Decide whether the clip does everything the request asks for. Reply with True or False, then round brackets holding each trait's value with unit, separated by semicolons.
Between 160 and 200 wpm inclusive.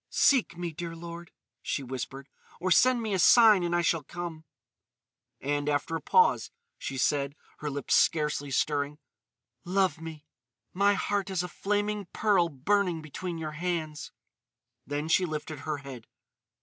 False (150 wpm)